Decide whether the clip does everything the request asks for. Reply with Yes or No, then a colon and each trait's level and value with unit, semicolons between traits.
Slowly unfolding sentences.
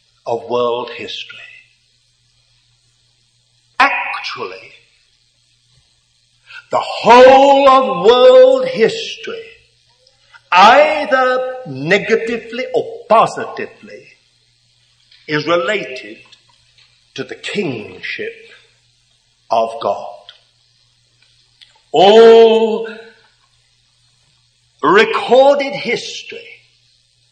Yes: slow, 50 wpm